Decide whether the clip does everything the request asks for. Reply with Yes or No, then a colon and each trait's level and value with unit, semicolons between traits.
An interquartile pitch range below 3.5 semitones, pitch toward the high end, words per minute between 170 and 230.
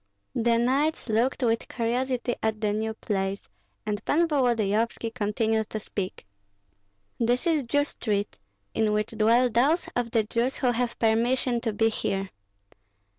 No: narrow, 2.5 semitones; high, 230 Hz; average, 145 wpm